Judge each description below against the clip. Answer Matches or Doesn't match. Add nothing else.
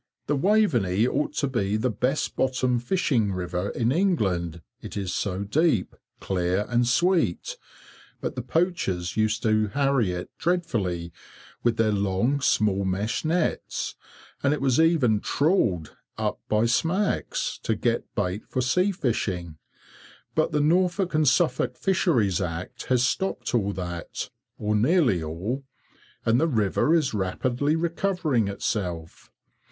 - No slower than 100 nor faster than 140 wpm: Matches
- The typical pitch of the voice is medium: Doesn't match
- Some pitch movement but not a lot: Doesn't match